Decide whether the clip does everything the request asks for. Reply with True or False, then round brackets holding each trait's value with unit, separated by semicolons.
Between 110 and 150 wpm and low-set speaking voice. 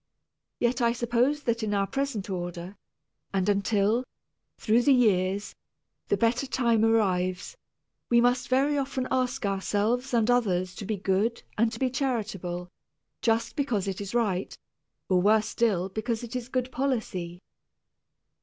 False (145 wpm; 225 Hz)